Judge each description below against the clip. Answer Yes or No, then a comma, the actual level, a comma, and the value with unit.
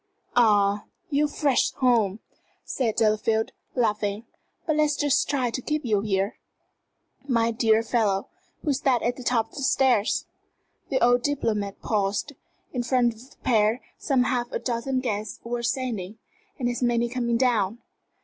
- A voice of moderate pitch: No, high, 235 Hz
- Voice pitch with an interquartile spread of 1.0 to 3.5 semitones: Yes, average, 3.0 semitones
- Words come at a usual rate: Yes, average, 160 wpm